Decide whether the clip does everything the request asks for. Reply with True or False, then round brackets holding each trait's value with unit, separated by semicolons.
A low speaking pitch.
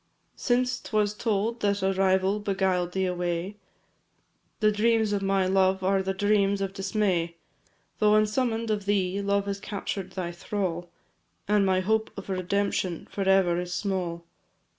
False (195 Hz)